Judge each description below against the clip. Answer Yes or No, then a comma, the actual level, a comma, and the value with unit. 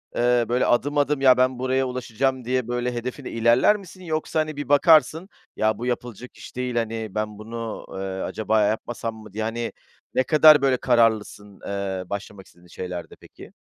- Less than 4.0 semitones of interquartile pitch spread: Yes, average, 3.2 semitones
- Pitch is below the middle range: Yes, low, 120 Hz